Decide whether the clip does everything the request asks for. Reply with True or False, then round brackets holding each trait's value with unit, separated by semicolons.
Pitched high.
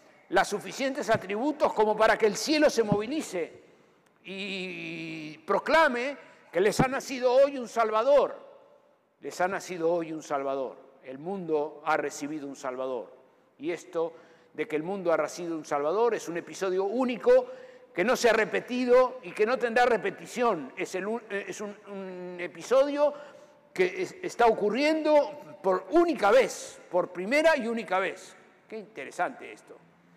True (210 Hz)